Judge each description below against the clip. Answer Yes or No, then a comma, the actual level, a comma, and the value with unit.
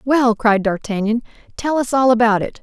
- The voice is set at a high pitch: Yes, high, 230 Hz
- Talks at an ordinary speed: Yes, average, 185 wpm